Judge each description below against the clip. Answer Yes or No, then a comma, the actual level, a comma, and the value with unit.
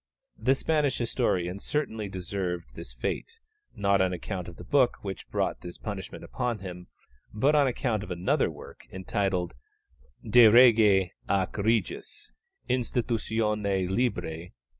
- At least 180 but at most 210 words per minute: No, slow, 135 wpm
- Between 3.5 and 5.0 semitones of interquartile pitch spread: Yes, average, 4.5 semitones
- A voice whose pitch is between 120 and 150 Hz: No, low, 100 Hz